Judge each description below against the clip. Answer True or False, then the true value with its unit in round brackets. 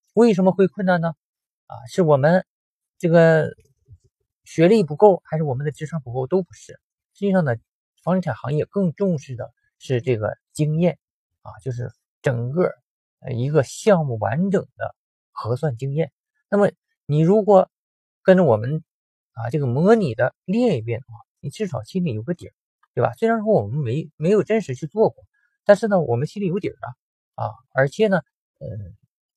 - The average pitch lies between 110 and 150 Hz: False (160 Hz)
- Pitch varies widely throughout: True (6.9 semitones)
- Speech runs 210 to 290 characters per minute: True (255 characters per minute)